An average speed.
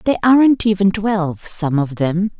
Yes: average, 175 wpm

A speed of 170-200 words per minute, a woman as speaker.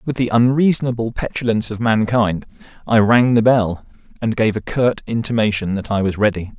No: average, 175 wpm; male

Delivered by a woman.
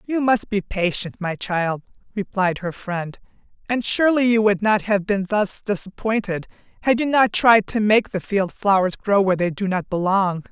Yes: female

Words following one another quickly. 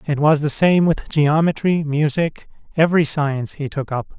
No: average, 170 wpm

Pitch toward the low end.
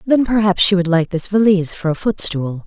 No: medium, 185 Hz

